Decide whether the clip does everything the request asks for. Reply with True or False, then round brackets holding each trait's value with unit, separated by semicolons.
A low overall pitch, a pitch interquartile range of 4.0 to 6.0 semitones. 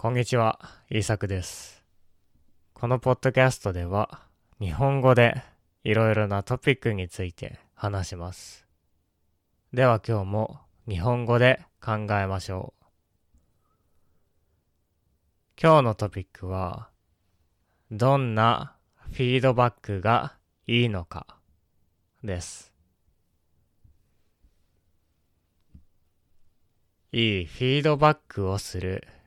True (100 Hz; 5.2 semitones)